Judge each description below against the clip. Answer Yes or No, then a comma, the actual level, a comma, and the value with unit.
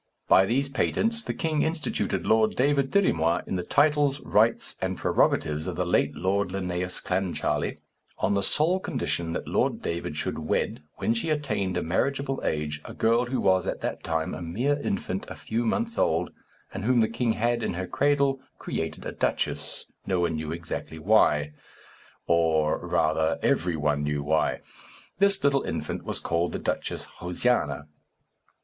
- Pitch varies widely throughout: Yes, wide, 8.6 semitones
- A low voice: Yes, very low, 95 Hz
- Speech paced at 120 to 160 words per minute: No, average, 170 wpm